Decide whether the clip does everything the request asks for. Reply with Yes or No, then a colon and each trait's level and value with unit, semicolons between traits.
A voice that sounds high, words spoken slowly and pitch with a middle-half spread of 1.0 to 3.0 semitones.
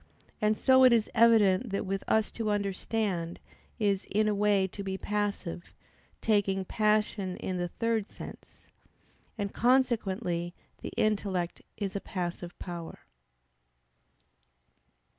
Yes: high, 200 Hz; slow, 120 wpm; narrow, 2.5 semitones